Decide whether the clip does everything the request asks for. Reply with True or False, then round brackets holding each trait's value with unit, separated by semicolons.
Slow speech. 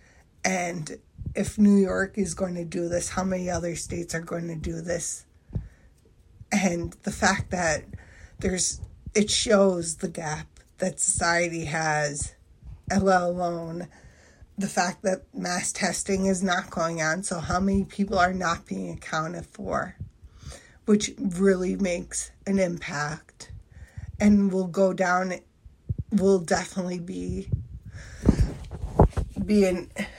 True (125 wpm)